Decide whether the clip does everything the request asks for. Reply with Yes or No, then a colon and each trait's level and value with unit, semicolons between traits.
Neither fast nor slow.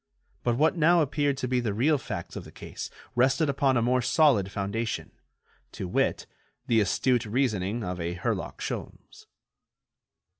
Yes: average, 155 wpm